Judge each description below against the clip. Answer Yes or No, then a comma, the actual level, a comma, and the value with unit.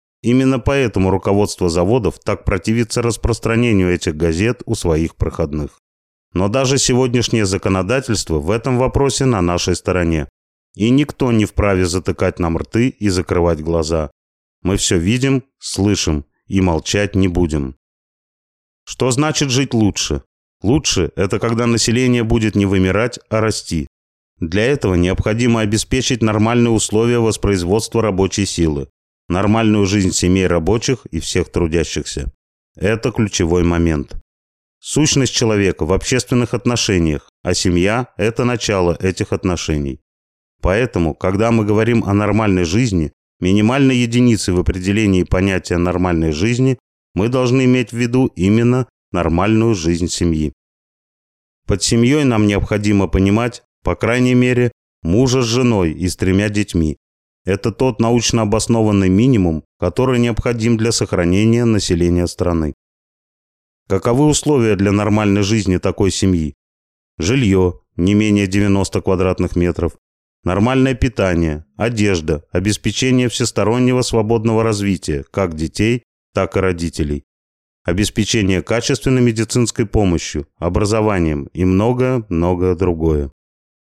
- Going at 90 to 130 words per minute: Yes, average, 120 wpm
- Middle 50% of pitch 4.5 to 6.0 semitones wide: Yes, average, 5.3 semitones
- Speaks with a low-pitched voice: Yes, low, 100 Hz